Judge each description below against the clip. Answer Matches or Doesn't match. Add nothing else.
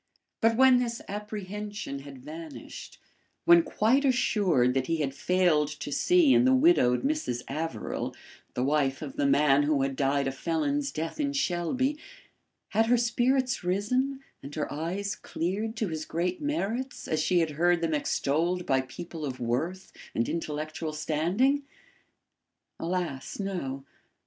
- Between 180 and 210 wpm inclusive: Doesn't match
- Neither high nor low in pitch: Matches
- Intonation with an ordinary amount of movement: Doesn't match